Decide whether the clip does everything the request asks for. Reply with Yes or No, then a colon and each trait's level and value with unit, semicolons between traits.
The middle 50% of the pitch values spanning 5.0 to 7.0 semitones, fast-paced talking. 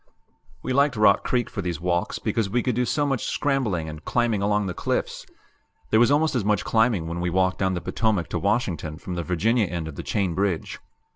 Yes: wide, 5.5 semitones; fast, 220 wpm